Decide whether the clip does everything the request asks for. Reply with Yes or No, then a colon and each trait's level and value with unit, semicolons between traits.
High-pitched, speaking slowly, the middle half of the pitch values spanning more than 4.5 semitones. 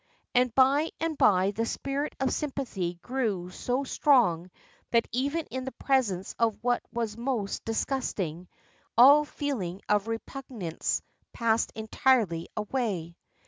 Yes: high, 235 Hz; slow, 125 wpm; average, 5.3 semitones